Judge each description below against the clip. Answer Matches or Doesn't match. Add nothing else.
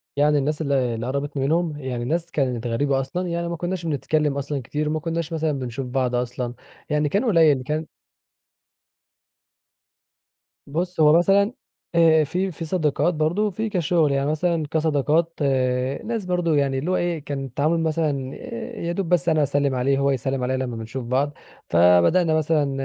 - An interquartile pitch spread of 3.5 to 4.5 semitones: Matches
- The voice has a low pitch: Doesn't match